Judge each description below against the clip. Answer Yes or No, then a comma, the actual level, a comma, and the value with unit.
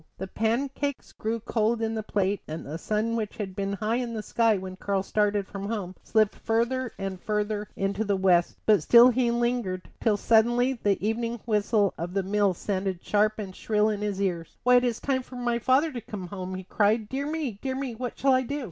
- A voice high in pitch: Yes, high, 215 Hz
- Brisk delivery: Yes, fast, 220 wpm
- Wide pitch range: No, average, 3.3 semitones